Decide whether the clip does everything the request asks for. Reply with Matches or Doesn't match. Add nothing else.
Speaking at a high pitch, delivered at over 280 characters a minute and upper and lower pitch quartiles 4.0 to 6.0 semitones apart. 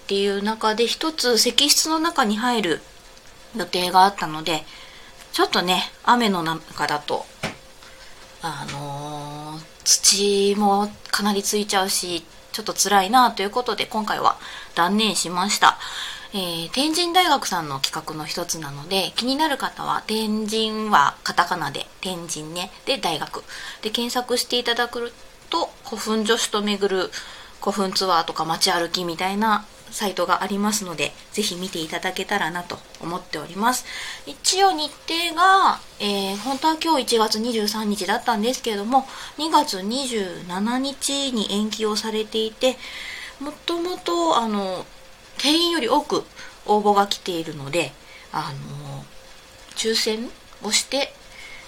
Doesn't match